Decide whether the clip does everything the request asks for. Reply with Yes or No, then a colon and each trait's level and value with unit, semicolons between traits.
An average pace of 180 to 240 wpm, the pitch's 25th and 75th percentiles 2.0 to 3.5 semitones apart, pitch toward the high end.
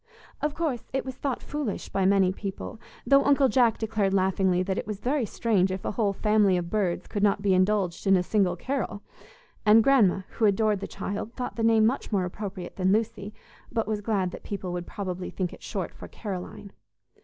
Yes: fast, 205 wpm; average, 3.1 semitones; high, 205 Hz